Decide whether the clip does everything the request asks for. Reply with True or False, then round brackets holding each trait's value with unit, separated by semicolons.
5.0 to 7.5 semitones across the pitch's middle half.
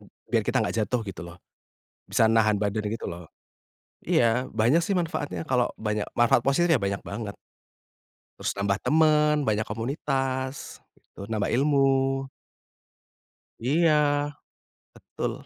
True (5.3 semitones)